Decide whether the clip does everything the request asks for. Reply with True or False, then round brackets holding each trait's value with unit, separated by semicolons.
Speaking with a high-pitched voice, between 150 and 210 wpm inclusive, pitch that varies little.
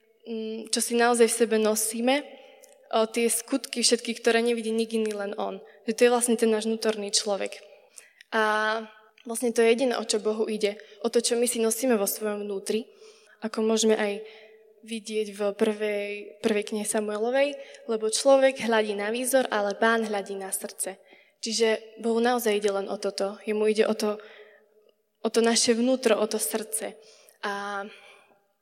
True (220 Hz; 170 wpm; 1.7 semitones)